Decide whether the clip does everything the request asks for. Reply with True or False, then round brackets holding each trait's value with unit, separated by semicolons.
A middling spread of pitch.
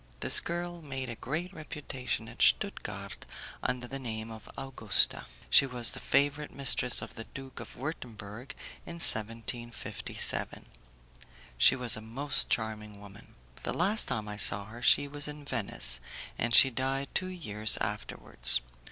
True (4.6 semitones)